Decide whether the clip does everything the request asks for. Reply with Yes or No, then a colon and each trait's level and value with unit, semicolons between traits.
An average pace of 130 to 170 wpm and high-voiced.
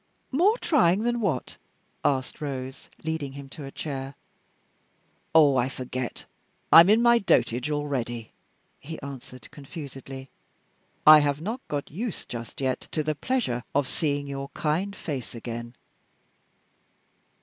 No: slow, 135 wpm; medium, 140 Hz